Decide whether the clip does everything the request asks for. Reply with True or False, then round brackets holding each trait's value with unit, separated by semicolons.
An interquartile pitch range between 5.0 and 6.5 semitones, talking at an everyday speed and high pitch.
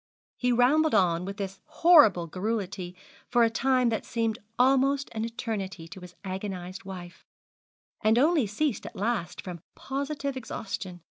True (5.6 semitones; 145 wpm; 220 Hz)